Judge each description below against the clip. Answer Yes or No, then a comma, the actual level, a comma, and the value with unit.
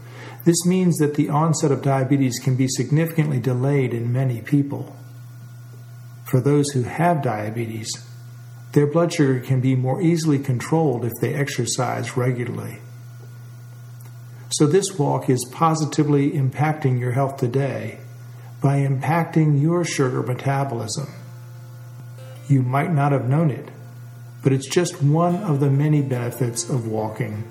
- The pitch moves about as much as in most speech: Yes, average, 3.2 semitones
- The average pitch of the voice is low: Yes, low, 130 Hz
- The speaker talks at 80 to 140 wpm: Yes, slow, 135 wpm